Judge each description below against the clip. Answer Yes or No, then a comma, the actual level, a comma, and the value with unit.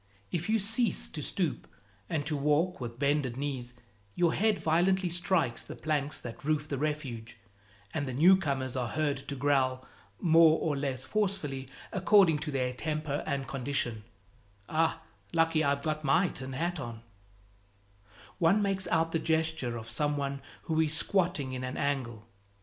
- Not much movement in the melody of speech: No, average, 3.8 semitones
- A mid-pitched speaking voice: Yes, medium, 150 Hz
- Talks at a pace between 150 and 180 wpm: Yes, average, 160 wpm